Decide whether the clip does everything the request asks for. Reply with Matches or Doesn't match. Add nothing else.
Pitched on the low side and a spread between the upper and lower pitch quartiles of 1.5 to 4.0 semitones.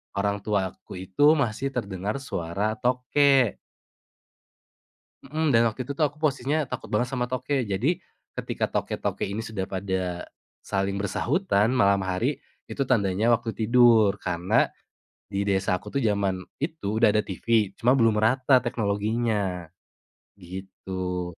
Doesn't match